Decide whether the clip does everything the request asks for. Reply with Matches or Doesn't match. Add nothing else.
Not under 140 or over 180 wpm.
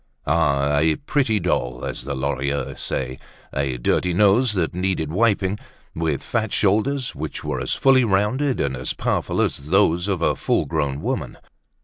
Matches